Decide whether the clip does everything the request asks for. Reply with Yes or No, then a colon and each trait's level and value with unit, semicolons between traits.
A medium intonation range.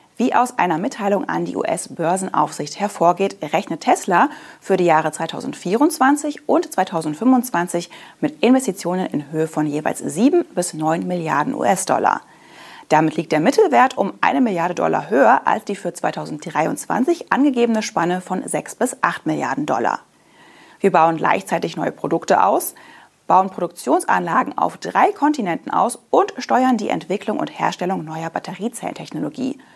No: wide, 7.6 semitones